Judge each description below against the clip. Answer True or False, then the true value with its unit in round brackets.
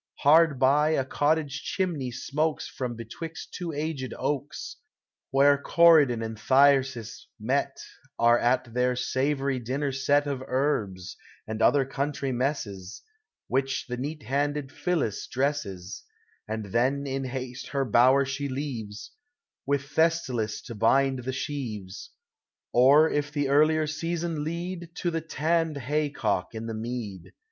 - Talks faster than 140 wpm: False (135 wpm)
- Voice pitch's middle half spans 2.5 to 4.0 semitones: True (3.4 semitones)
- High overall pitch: False (135 Hz)